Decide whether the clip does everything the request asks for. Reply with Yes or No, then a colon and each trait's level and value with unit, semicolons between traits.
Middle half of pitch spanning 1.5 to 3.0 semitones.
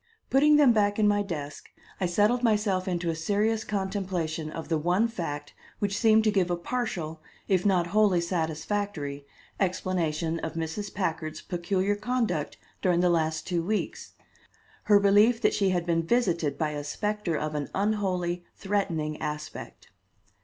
No: average, 4.2 semitones